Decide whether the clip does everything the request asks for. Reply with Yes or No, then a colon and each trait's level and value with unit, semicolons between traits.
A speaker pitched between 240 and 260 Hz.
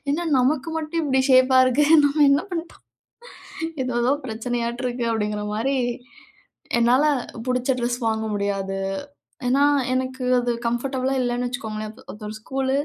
Yes: very high, 250 Hz